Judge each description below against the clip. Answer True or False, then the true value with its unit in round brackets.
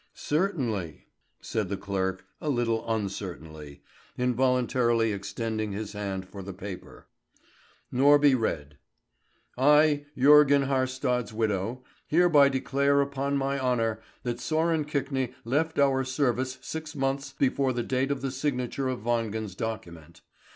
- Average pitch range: True (4.5 semitones)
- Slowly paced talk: True (125 wpm)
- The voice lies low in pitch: True (125 Hz)